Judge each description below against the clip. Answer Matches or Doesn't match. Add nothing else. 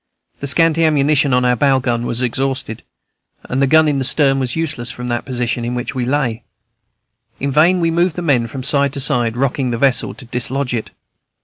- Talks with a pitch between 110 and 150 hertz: Matches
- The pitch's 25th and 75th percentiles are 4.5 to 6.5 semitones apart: Doesn't match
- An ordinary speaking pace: Doesn't match